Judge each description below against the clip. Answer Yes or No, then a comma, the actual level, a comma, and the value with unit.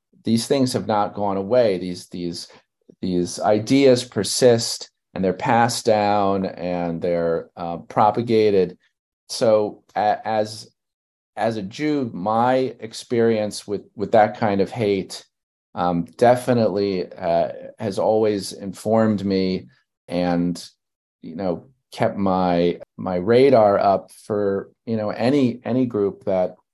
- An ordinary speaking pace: No, slow, 120 wpm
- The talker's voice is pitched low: Yes, low, 105 Hz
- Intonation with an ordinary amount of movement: Yes, average, 4.0 semitones